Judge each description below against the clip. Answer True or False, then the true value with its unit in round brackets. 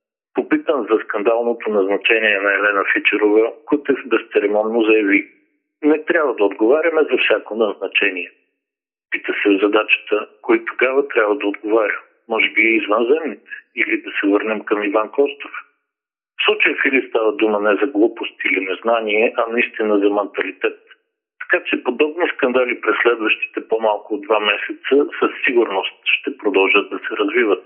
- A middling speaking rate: True (150 wpm)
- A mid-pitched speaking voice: True (150 Hz)